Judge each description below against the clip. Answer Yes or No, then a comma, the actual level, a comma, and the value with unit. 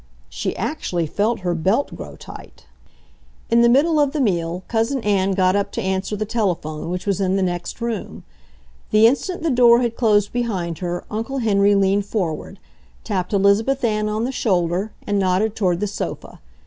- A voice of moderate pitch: No, high, 205 Hz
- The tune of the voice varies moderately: Yes, average, 3.8 semitones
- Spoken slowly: No, average, 180 wpm